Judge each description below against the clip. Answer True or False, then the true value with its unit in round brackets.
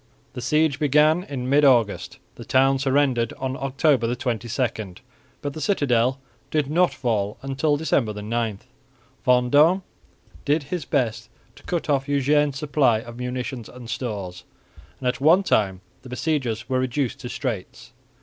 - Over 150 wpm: False (145 wpm)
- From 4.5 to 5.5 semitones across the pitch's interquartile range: False (3.6 semitones)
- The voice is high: False (130 Hz)